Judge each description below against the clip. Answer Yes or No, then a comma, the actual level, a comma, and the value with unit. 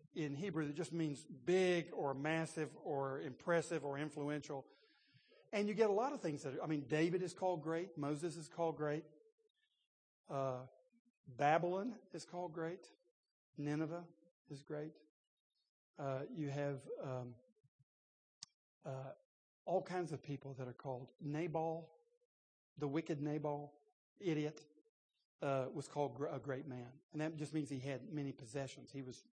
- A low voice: No, medium, 150 Hz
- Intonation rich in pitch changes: No, average, 3.2 semitones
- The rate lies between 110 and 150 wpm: Yes, average, 145 wpm